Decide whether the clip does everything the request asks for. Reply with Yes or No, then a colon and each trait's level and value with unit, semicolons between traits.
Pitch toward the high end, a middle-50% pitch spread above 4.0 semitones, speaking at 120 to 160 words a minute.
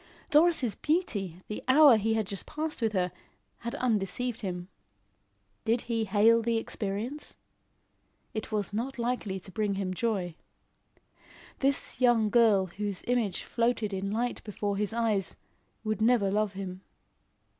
No: high, 220 Hz; average, 3.2 semitones; average, 140 wpm